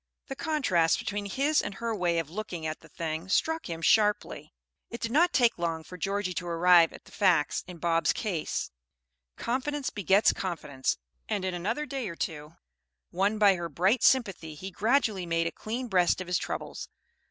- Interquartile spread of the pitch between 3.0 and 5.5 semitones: Yes, average, 5.2 semitones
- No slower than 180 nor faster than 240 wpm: Yes, average, 185 wpm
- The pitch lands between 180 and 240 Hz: Yes, high, 190 Hz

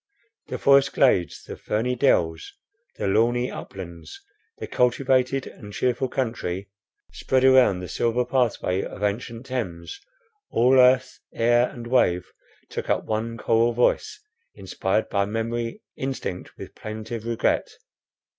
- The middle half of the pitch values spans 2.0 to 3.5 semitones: No, average, 3.9 semitones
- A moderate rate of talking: No, slow, 125 wpm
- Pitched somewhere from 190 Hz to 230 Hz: No, low, 115 Hz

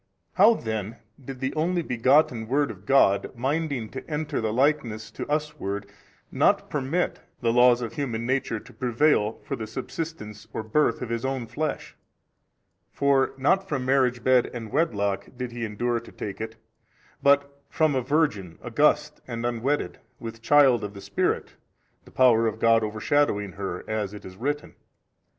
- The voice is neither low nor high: No, low, 125 Hz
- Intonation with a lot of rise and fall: No, average, 4.6 semitones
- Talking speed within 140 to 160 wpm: No, average, 170 wpm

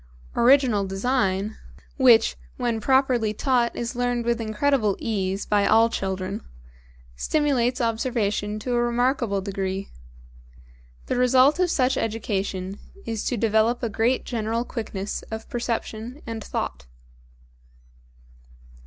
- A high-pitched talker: Yes, high, 230 Hz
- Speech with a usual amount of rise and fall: Yes, average, 3.2 semitones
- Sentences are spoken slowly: Yes, slow, 115 wpm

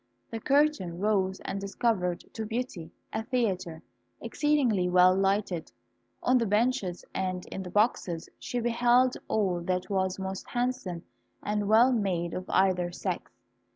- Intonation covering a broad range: No, average, 4.5 semitones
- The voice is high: Yes, high, 195 Hz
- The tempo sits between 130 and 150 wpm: Yes, average, 140 wpm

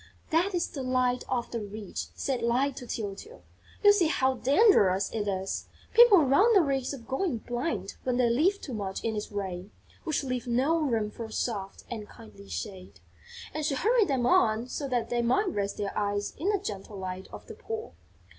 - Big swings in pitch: Yes, wide, 6.8 semitones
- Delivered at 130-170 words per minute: No, average, 195 wpm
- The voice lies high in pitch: Yes, high, 245 Hz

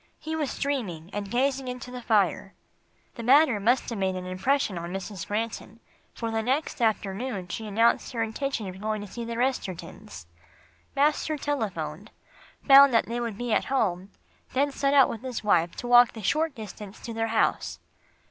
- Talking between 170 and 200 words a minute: Yes, average, 185 wpm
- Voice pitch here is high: Yes, high, 225 Hz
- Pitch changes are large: No, average, 4.7 semitones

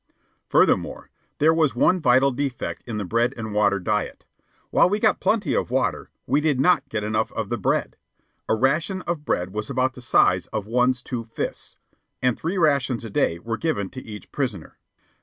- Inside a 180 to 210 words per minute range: Yes, average, 190 wpm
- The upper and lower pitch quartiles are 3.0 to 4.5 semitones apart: No, average, 5.0 semitones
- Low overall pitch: Yes, low, 125 Hz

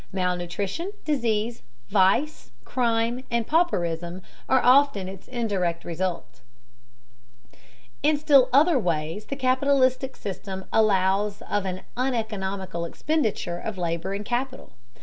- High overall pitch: Yes, high, 210 Hz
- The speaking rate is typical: No, slow, 110 wpm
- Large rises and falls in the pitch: Yes, wide, 5.7 semitones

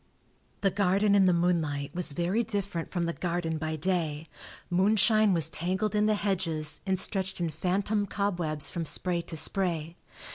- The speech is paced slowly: No, average, 160 wpm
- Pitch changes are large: No, average, 3.4 semitones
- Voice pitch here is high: No, medium, 180 Hz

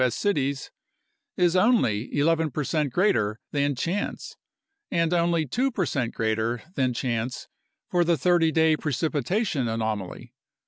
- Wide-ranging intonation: Yes, wide, 6.0 semitones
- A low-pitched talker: No, medium, 150 Hz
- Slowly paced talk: Yes, slow, 125 wpm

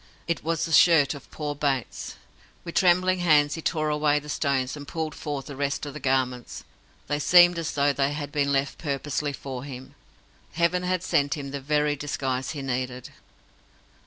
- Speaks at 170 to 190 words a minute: Yes, average, 185 wpm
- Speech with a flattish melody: Yes, narrow, 2.3 semitones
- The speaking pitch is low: No, medium, 145 Hz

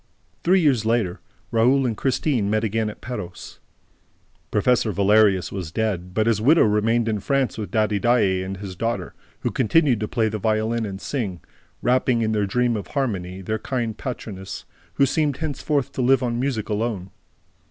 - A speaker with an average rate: Yes, average, 175 wpm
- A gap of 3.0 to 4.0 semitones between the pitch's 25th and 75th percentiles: Yes, average, 3.5 semitones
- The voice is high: No, low, 110 Hz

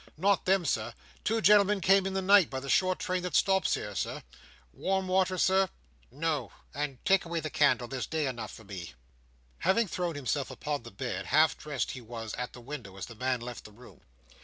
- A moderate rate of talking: No, fast, 210 wpm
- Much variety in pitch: Yes, wide, 7.5 semitones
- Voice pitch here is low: No, medium, 150 Hz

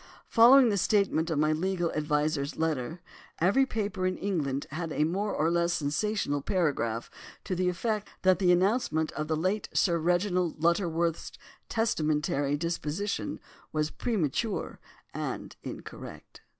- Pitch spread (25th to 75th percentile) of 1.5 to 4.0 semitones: No, average, 4.4 semitones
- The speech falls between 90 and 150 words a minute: Yes, slow, 135 wpm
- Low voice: No, medium, 170 Hz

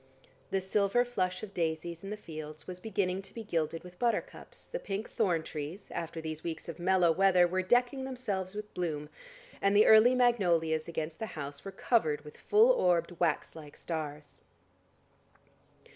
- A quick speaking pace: No, average, 170 wpm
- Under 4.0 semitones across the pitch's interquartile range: No, average, 4.6 semitones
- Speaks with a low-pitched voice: No, medium, 180 Hz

